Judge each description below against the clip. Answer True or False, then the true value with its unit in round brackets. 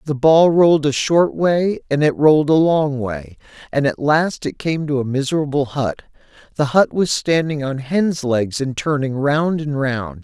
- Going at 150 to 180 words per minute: False (195 wpm)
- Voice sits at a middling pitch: True (145 Hz)